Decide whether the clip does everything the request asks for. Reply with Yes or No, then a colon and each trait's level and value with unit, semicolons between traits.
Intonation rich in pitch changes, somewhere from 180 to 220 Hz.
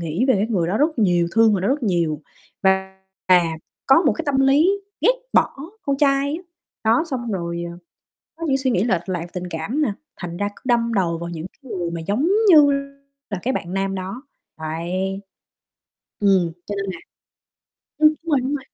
Yes: wide, 7.3 semitones; high, 200 Hz